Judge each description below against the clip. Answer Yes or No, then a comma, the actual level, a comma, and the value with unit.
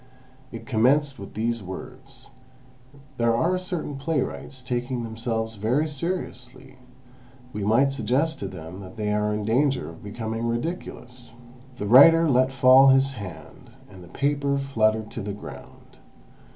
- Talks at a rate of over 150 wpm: No, average, 145 wpm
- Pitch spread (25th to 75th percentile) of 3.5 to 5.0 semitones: Yes, average, 4.1 semitones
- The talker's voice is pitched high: No, low, 125 Hz